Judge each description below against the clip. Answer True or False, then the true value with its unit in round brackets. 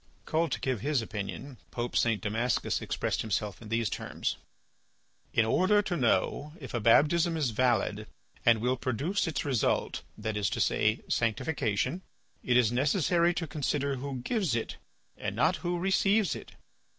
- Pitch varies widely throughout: True (6.2 semitones)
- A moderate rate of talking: True (160 wpm)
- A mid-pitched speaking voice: False (130 Hz)